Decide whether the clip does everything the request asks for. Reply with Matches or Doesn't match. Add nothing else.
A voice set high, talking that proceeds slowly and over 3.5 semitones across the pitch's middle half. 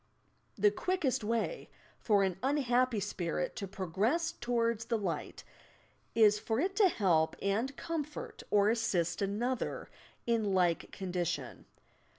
Matches